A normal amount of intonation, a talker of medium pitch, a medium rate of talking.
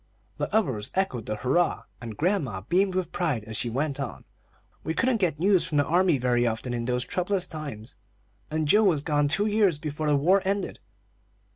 No: wide, 7.0 semitones; medium, 150 Hz; average, 190 wpm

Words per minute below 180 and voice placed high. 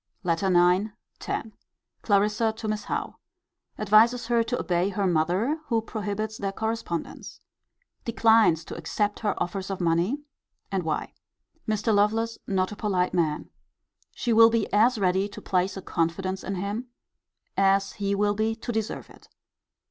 Yes: average, 150 wpm; high, 205 Hz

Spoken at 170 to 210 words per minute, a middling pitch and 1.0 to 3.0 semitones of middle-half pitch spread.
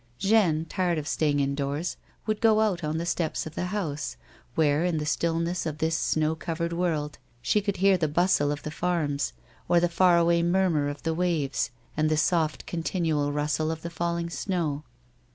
Yes: average, 190 wpm; medium, 165 Hz; narrow, 2.6 semitones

